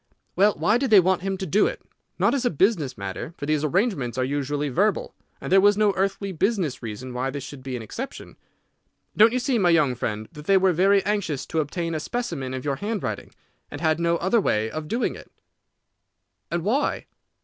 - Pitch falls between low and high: Yes, medium, 170 Hz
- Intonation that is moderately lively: No, wide, 6.5 semitones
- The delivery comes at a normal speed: No, fast, 210 wpm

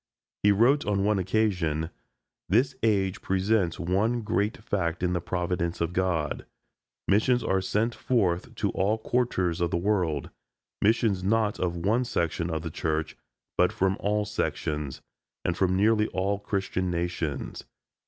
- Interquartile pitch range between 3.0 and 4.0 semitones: Yes, average, 3.6 semitones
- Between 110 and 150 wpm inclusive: Yes, average, 145 wpm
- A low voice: Yes, very low, 95 Hz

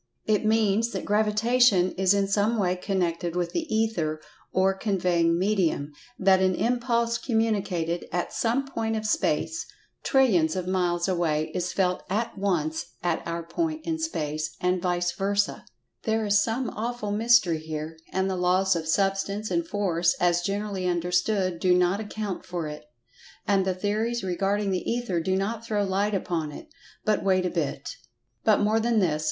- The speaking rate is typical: Yes, average, 165 wpm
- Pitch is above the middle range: Yes, high, 195 Hz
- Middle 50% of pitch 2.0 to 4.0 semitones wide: Yes, average, 3.6 semitones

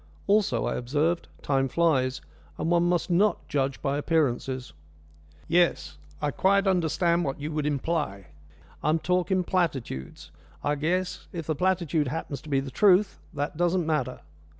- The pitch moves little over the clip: No, average, 4.2 semitones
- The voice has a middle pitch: Yes, medium, 160 Hz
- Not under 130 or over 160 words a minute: Yes, average, 150 wpm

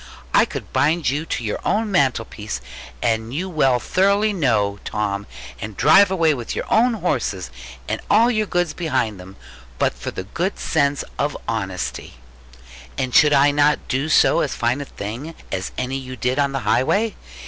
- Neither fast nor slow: Yes, average, 170 wpm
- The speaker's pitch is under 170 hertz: Yes, medium, 140 Hz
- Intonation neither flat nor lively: No, wide, 6.5 semitones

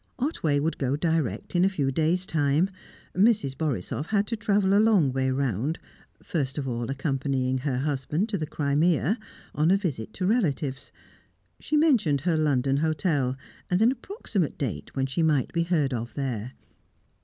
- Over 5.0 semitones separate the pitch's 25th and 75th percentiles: Yes, wide, 5.5 semitones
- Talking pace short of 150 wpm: No, average, 165 wpm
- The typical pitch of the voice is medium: Yes, medium, 150 Hz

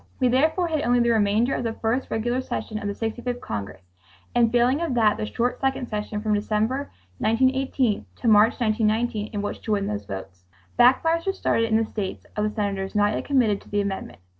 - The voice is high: Yes, high, 225 Hz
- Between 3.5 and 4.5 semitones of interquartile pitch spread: No, average, 3.1 semitones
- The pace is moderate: No, fast, 210 wpm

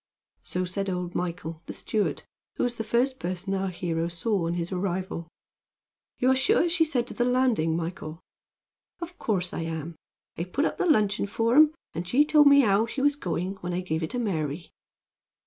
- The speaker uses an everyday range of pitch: No, wide, 6.4 semitones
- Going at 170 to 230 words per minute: Yes, average, 200 wpm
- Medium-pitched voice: No, high, 195 Hz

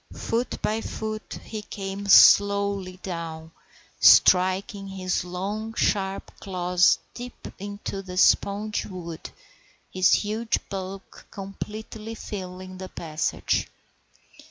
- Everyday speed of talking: No, slow, 100 wpm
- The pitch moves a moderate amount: No, narrow, 2.2 semitones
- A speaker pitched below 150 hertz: No, high, 195 Hz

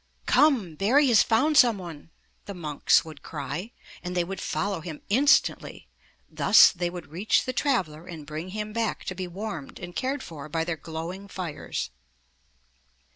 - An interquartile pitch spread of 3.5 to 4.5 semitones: No, average, 5.0 semitones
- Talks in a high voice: No, medium, 180 Hz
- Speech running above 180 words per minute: No, average, 165 wpm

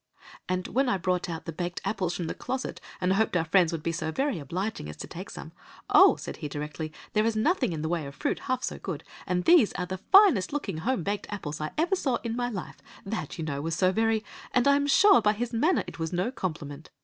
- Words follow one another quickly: Yes, fast, 250 wpm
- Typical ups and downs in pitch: No, wide, 6.9 semitones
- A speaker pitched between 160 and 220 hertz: Yes, medium, 185 Hz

